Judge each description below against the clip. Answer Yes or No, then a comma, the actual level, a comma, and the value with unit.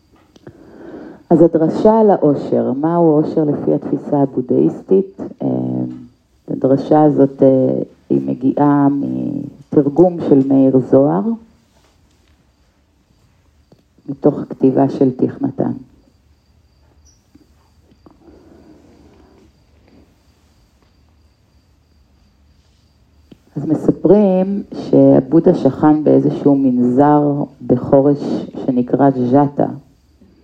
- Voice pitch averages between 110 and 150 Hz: Yes, low, 135 Hz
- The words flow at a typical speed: No, slow, 60 wpm